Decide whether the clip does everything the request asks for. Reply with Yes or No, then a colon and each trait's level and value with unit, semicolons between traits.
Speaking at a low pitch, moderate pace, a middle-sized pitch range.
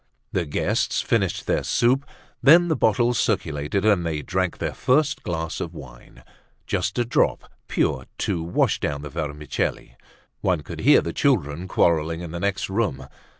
No: very low, 85 Hz; average, 160 wpm; wide, 6.4 semitones